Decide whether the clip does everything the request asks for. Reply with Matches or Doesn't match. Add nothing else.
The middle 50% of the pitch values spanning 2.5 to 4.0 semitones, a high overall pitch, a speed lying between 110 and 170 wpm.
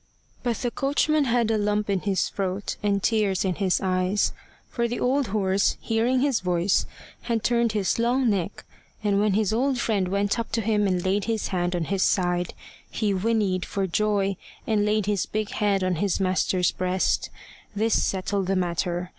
Doesn't match